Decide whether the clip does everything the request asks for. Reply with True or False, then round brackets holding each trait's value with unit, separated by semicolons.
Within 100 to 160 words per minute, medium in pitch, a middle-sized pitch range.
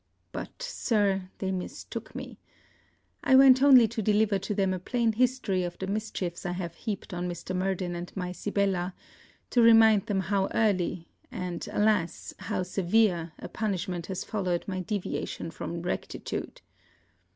False (150 wpm; 195 Hz; 3.4 semitones)